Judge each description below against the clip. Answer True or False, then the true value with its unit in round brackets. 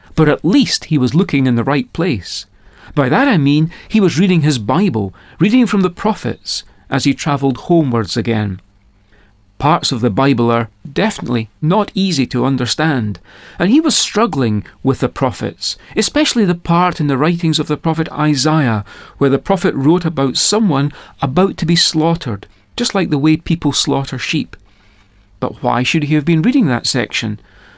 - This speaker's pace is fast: False (175 wpm)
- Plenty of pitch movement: True (6.4 semitones)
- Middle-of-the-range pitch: True (145 Hz)